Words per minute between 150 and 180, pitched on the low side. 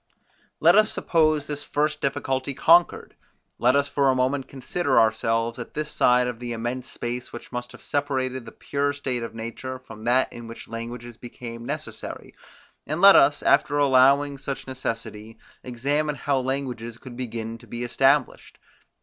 Yes: average, 165 wpm; low, 130 Hz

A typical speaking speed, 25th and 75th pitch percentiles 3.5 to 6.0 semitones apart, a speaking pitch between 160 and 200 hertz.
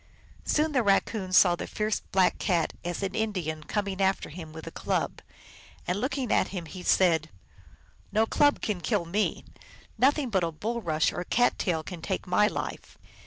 Yes: average, 180 wpm; average, 4.1 semitones; high, 190 Hz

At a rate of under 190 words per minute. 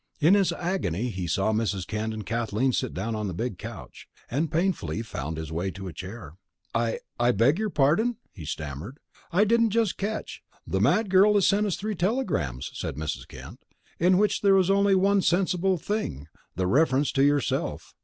No: average, 195 wpm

